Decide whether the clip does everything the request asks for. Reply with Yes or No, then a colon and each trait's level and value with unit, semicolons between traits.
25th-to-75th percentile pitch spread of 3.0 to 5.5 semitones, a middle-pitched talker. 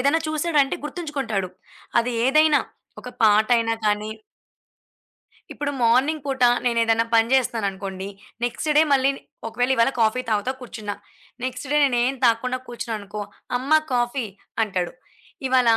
No: average, 3.5 semitones; high, 240 Hz